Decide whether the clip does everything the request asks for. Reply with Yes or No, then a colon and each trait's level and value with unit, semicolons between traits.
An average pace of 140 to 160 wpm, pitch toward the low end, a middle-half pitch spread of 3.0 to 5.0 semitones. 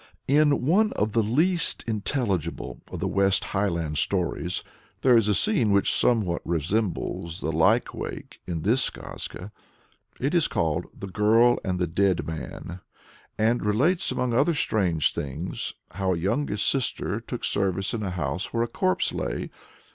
No: average, 155 wpm; low, 100 Hz; wide, 5.5 semitones